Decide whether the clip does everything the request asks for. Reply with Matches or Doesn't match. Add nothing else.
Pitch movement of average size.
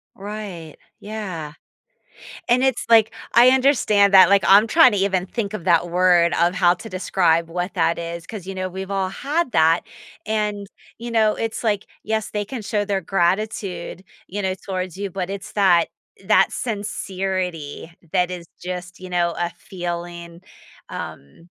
Matches